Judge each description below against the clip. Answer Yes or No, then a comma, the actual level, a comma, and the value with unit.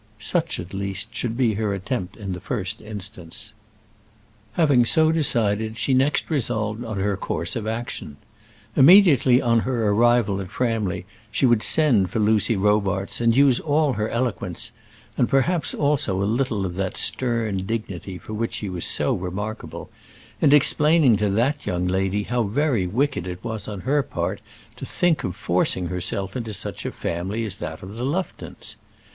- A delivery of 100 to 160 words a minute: No, average, 170 wpm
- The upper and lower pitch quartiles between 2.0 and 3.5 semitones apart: No, average, 4.8 semitones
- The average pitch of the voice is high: No, low, 110 Hz